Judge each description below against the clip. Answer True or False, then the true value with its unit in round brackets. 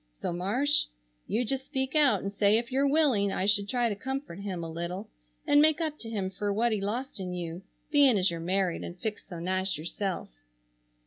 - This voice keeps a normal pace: False (210 wpm)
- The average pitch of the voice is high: True (205 Hz)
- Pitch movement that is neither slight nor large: False (6.1 semitones)